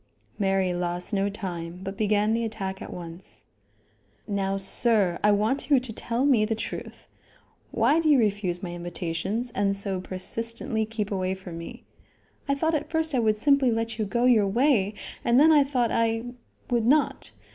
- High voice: Yes, high, 215 Hz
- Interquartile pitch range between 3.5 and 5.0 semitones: Yes, average, 3.9 semitones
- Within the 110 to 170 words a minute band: No, average, 180 wpm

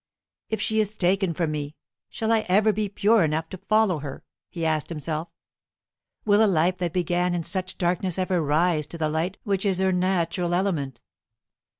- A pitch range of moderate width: Yes, average, 3.2 semitones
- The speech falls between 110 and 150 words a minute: No, average, 185 wpm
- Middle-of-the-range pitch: Yes, medium, 180 Hz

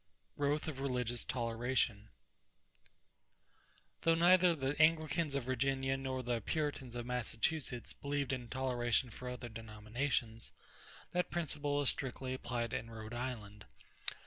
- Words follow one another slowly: Yes, slow, 120 wpm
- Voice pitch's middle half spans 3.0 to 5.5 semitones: Yes, average, 3.3 semitones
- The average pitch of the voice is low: Yes, low, 130 Hz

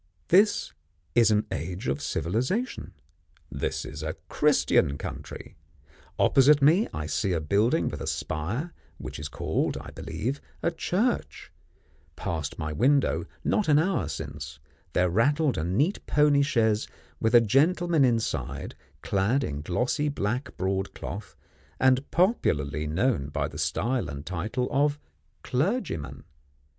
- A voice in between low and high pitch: No, low, 115 Hz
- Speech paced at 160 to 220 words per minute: No, slow, 135 wpm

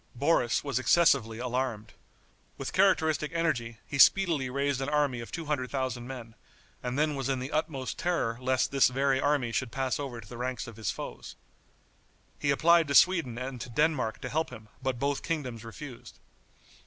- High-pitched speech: No, low, 135 Hz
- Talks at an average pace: Yes, average, 180 wpm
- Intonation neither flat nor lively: Yes, average, 3.4 semitones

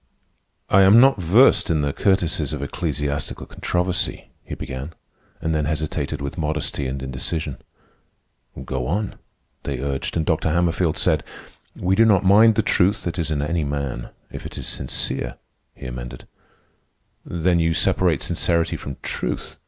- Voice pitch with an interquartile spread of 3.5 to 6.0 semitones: Yes, average, 4.3 semitones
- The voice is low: Yes, very low, 80 Hz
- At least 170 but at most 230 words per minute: No, average, 155 wpm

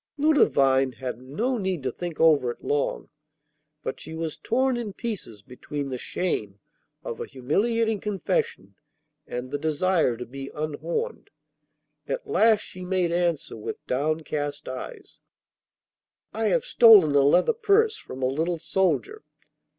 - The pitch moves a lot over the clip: Yes, wide, 8.2 semitones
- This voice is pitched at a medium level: Yes, medium, 160 Hz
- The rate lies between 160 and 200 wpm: No, average, 140 wpm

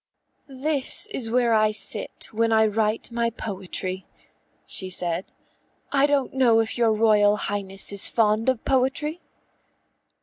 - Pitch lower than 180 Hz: No, high, 225 Hz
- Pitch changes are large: No, average, 3.6 semitones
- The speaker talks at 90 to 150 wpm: Yes, slow, 135 wpm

